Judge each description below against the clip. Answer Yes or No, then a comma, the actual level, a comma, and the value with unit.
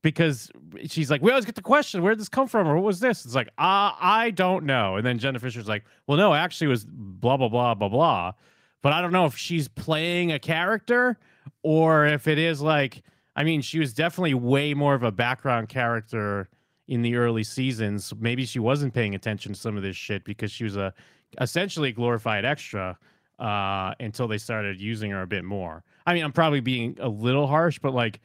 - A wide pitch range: Yes, wide, 6.4 semitones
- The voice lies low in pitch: Yes, low, 130 Hz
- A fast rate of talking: Yes, fast, 220 wpm